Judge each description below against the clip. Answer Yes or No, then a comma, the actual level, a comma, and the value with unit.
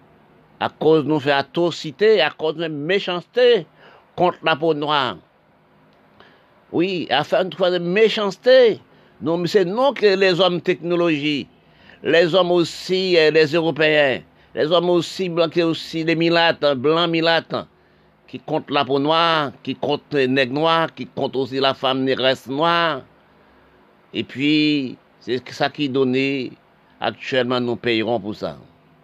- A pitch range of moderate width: Yes, average, 4.1 semitones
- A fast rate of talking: No, slow, 145 wpm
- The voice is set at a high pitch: No, medium, 160 Hz